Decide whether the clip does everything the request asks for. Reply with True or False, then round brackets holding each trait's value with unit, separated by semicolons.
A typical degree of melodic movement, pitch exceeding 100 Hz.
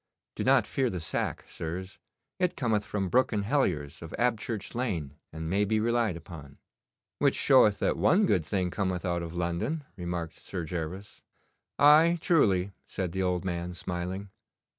False (4.6 semitones; 95 Hz)